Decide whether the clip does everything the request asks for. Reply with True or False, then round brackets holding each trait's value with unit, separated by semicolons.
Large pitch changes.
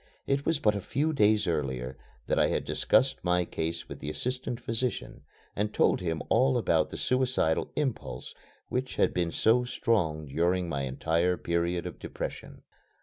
True (7.4 semitones)